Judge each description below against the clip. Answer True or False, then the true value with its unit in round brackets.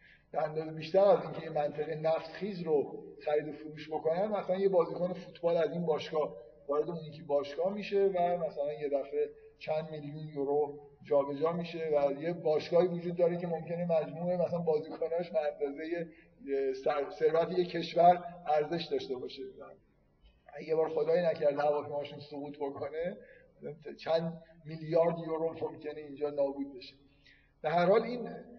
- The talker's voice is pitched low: False (160 Hz)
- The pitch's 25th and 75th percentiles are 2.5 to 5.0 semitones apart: True (2.9 semitones)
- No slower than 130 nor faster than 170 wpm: True (145 wpm)